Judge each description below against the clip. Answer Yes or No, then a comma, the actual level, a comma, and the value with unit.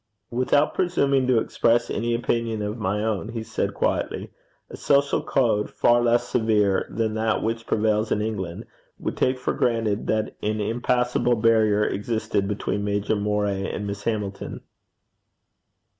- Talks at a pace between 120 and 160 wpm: Yes, average, 145 wpm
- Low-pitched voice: Yes, low, 110 Hz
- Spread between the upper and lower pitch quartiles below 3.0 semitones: Yes, narrow, 2.4 semitones